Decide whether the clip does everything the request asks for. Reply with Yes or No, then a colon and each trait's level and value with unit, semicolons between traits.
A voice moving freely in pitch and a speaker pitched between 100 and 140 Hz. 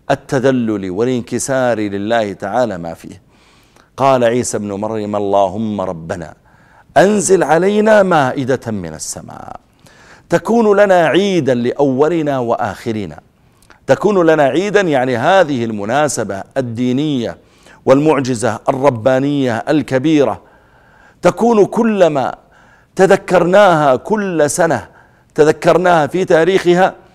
Yes: wide, 7.2 semitones; low, 135 Hz